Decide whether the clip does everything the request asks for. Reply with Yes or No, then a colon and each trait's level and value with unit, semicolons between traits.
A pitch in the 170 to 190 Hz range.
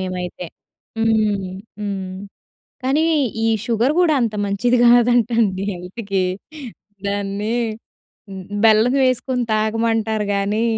No: high, 215 Hz